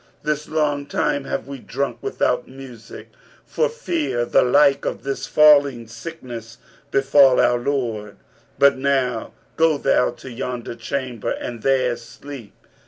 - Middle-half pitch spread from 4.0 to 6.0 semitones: No, average, 3.0 semitones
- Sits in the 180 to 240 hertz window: No, low, 135 Hz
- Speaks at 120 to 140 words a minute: Yes, slow, 135 wpm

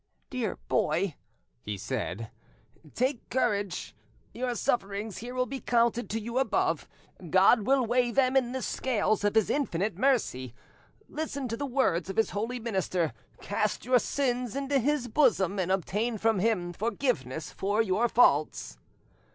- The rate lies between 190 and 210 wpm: No, average, 150 wpm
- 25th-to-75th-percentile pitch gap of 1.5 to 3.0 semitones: No, average, 4.8 semitones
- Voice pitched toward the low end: No, high, 225 Hz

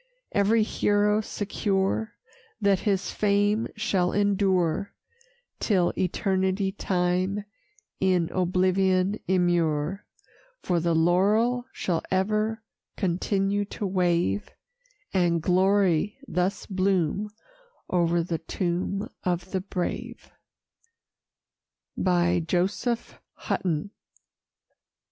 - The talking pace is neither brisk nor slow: No, slow, 80 wpm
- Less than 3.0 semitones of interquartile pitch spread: Yes, narrow, 2.4 semitones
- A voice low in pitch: No, high, 190 Hz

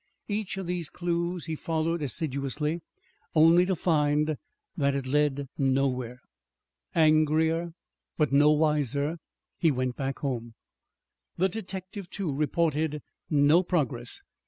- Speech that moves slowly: Yes, slow, 115 wpm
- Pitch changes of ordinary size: Yes, average, 3.3 semitones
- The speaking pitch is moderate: Yes, medium, 155 Hz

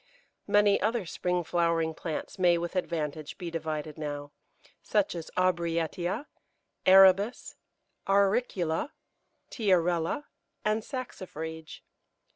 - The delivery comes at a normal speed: No, slow, 90 wpm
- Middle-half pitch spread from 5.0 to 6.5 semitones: No, average, 3.4 semitones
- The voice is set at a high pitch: No, medium, 175 Hz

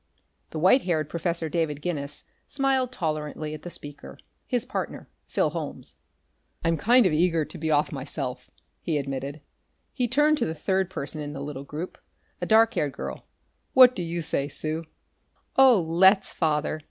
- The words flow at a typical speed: Yes, average, 165 wpm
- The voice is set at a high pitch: No, medium, 165 Hz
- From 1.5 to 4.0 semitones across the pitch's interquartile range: No, average, 4.4 semitones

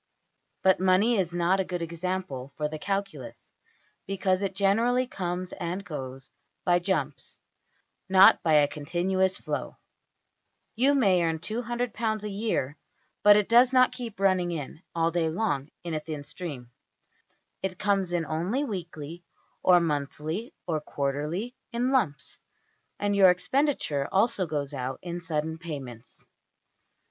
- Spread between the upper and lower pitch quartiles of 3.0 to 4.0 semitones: No, average, 4.4 semitones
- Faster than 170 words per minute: No, average, 140 wpm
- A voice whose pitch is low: No, medium, 180 Hz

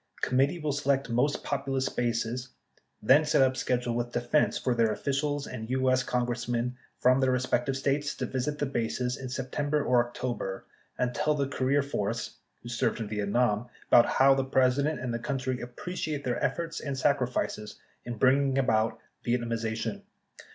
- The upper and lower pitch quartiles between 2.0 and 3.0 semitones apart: Yes, narrow, 2.5 semitones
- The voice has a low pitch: Yes, low, 130 Hz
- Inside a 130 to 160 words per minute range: No, average, 170 wpm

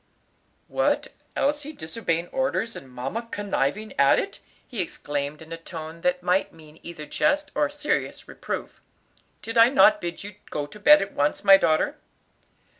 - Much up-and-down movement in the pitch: Yes, wide, 6.4 semitones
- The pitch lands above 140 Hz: Yes, medium, 185 Hz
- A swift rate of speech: No, average, 160 wpm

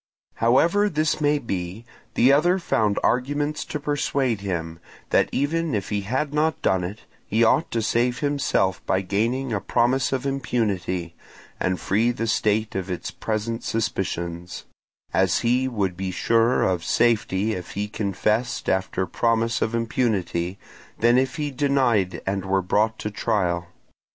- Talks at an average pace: Yes, average, 150 wpm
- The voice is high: No, low, 115 Hz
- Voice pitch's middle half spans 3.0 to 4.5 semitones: No, average, 5.3 semitones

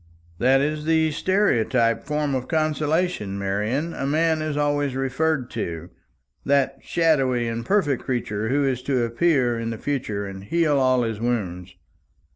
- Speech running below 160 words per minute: Yes, average, 150 wpm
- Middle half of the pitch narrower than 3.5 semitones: No, average, 4.9 semitones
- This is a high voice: No, low, 135 Hz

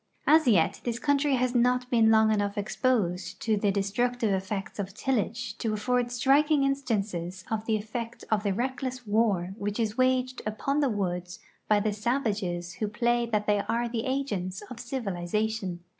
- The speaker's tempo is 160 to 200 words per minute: Yes, average, 175 wpm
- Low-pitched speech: No, high, 220 Hz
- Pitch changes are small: No, average, 3.6 semitones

